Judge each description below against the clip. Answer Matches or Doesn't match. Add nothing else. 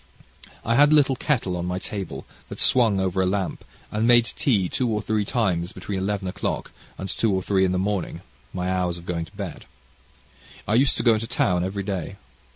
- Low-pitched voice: Matches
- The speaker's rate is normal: Doesn't match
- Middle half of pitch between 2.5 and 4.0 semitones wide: Matches